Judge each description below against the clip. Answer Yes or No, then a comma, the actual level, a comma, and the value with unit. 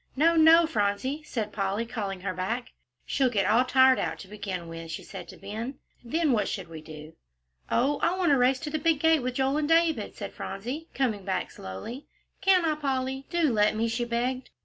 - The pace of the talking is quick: Yes, fast, 210 wpm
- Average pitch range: No, wide, 6.5 semitones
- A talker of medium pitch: No, very high, 250 Hz